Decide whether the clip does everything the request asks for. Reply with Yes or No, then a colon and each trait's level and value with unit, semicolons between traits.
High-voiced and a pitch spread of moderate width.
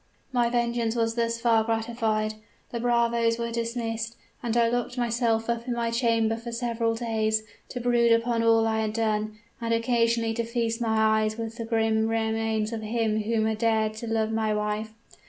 No: high, 230 Hz; narrow, 1.0 semitones